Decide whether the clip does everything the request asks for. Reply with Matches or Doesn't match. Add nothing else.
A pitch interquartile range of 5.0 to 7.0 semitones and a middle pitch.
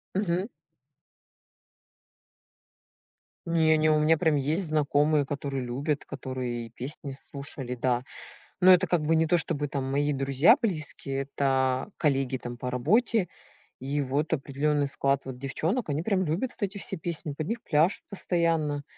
Doesn't match